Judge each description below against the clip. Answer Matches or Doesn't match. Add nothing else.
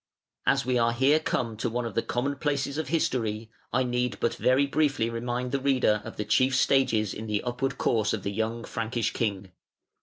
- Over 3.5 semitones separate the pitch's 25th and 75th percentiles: Doesn't match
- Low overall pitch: Matches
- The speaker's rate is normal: Doesn't match